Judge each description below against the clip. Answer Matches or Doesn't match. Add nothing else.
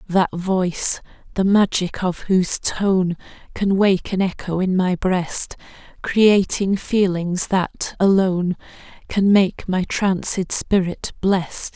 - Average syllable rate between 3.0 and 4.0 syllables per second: Matches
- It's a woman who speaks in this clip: Matches